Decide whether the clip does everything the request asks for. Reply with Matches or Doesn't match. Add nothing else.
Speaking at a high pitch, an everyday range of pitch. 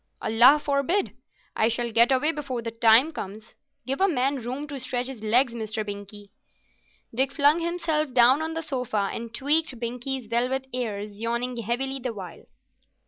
Matches